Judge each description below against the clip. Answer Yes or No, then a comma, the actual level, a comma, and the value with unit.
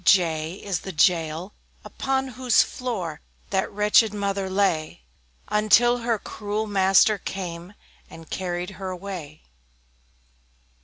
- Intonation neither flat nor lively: Yes, average, 3.2 semitones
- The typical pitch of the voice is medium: No, high, 195 Hz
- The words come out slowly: Yes, slow, 115 wpm